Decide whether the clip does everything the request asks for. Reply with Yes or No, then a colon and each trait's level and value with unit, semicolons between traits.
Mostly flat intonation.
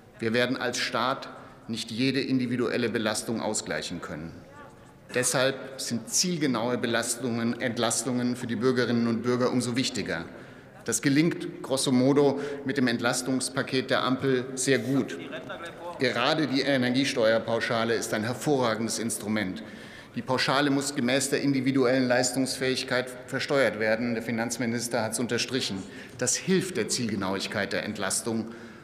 Yes: narrow, 2.2 semitones